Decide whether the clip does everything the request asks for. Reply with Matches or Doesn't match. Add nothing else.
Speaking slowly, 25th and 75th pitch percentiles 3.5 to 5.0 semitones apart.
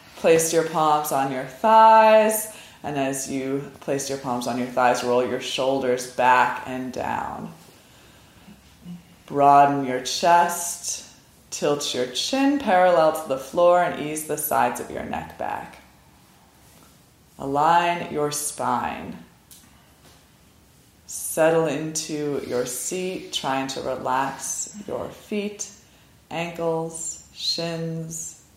Matches